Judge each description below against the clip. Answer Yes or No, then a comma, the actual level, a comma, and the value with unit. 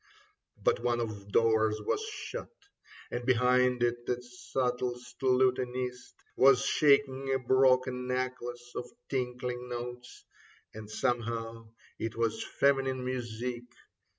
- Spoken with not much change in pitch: Yes, narrow, 1.3 semitones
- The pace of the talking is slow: Yes, slow, 115 wpm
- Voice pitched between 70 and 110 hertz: No, low, 125 Hz